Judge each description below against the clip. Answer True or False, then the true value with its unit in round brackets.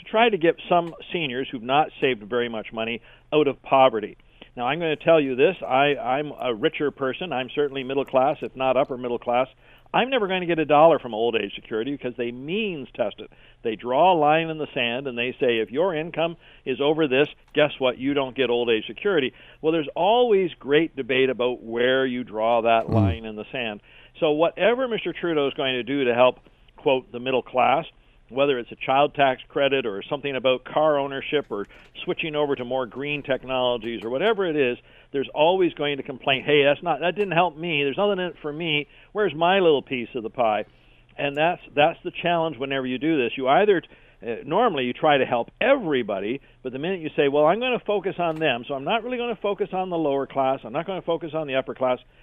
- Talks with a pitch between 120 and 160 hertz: True (140 Hz)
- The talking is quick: True (230 wpm)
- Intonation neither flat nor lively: True (4.3 semitones)